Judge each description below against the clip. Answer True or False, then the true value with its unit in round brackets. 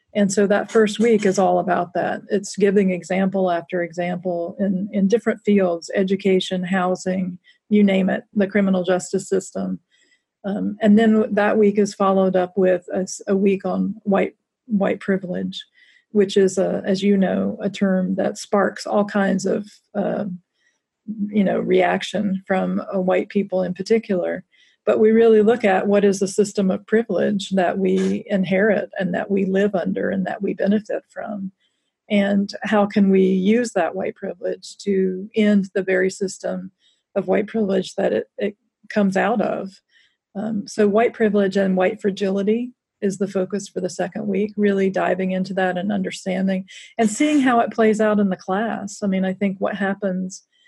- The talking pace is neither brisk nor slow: True (175 wpm)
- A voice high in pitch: True (195 Hz)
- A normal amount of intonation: False (1.8 semitones)